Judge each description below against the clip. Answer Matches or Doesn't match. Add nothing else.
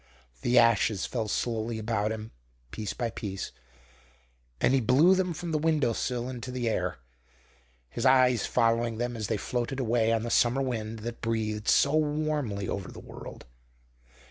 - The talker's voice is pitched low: Matches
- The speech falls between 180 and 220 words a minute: Doesn't match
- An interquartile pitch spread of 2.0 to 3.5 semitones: Matches